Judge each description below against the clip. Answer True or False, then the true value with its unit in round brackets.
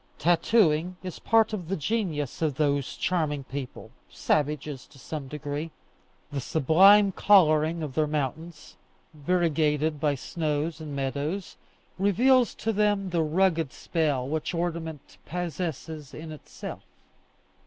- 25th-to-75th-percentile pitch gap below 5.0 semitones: True (3.4 semitones)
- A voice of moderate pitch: True (160 Hz)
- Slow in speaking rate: True (120 wpm)